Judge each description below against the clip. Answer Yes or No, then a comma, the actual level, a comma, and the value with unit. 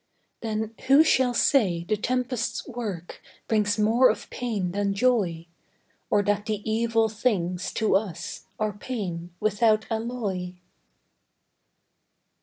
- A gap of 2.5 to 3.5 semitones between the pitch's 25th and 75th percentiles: Yes, average, 3.0 semitones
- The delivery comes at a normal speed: No, slow, 115 wpm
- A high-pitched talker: Yes, high, 215 Hz